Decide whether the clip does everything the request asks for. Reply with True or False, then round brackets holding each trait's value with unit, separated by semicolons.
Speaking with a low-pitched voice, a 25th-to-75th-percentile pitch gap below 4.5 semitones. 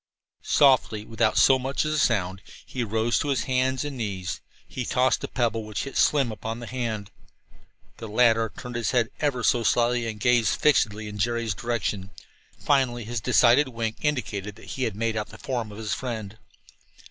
True (115 Hz; 2.8 semitones)